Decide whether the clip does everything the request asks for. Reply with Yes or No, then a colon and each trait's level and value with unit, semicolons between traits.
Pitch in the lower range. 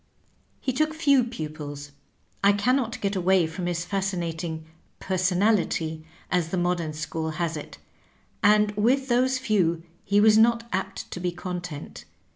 No: medium, 185 Hz